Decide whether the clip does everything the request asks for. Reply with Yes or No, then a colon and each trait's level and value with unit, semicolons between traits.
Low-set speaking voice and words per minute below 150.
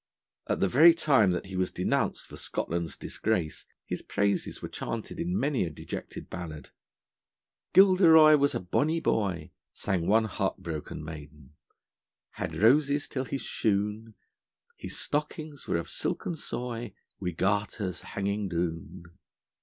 Yes: low, 105 Hz; average, 140 wpm